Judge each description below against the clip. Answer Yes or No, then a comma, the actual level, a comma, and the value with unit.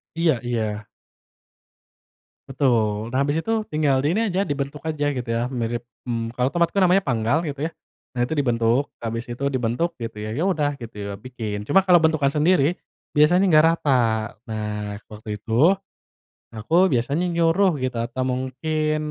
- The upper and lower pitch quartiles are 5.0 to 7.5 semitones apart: Yes, wide, 5.5 semitones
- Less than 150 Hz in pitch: Yes, low, 135 Hz